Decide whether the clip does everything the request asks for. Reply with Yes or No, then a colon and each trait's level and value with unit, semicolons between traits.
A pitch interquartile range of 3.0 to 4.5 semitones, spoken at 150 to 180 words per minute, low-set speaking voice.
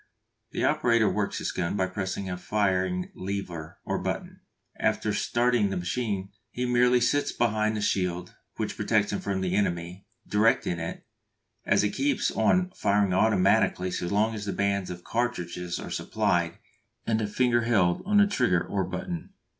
Yes: average, 4.2 semitones; average, 165 wpm; low, 100 Hz